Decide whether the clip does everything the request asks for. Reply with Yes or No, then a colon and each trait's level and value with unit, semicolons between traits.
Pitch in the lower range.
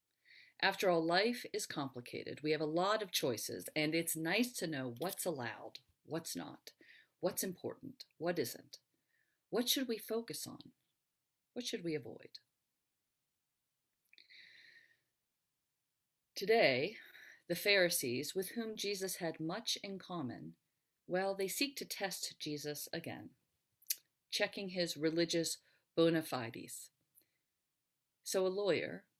No: medium, 185 Hz